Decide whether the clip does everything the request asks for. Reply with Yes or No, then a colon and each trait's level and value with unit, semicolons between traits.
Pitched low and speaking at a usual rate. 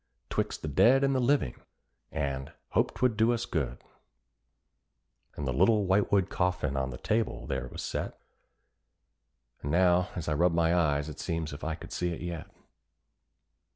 Yes: very low, 85 Hz; average, 170 wpm